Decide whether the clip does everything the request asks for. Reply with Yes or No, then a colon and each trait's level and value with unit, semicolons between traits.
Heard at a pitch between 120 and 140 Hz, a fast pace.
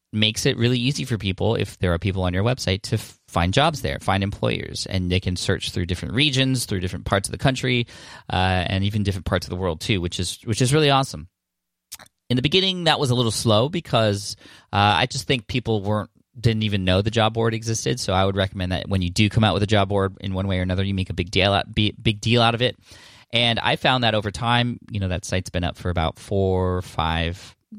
No: low, 105 Hz; fast, 250 wpm